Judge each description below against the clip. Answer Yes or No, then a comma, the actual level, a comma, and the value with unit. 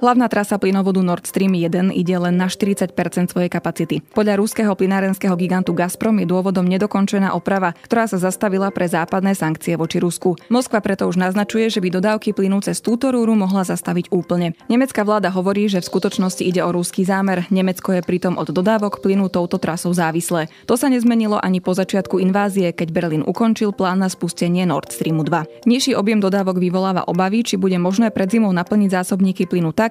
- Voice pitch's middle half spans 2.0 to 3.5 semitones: Yes, narrow, 2.5 semitones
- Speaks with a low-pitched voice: No, high, 190 Hz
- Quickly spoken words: Yes, fast, 185 wpm